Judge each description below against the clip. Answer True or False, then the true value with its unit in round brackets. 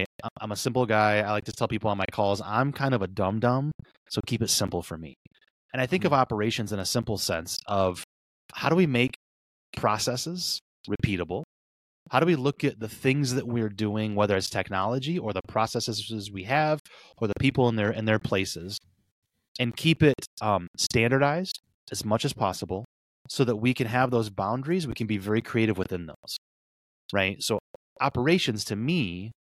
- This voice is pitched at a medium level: False (110 Hz)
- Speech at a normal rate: True (190 wpm)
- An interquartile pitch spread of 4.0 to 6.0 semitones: True (4.4 semitones)